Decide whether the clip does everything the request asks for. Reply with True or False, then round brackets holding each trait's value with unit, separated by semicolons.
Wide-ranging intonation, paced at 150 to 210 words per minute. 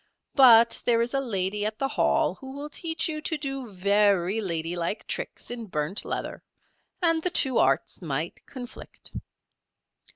True (6.4 semitones; 155 wpm)